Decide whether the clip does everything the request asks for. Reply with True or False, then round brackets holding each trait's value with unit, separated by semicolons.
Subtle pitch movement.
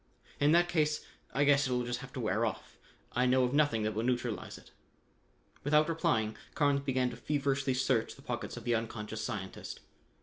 False (3.8 semitones)